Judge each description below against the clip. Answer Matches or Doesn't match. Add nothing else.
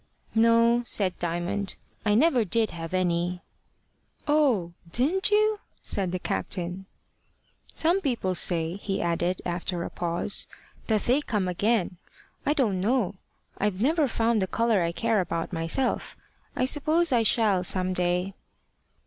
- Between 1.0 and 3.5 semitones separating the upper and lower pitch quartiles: Doesn't match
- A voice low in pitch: Doesn't match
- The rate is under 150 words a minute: Matches